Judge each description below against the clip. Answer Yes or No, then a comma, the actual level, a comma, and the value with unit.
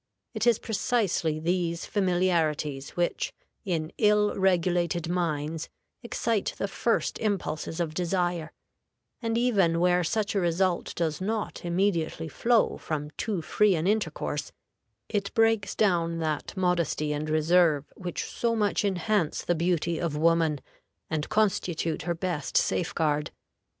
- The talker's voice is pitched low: No, medium, 175 Hz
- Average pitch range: Yes, average, 3.9 semitones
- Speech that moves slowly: Yes, slow, 130 wpm